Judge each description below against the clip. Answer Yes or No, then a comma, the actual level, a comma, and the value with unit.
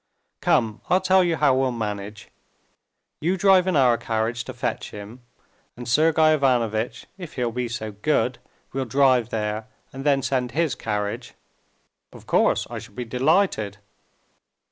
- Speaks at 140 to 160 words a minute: Yes, average, 150 wpm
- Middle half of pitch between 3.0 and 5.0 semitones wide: No, wide, 5.4 semitones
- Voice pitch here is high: No, low, 125 Hz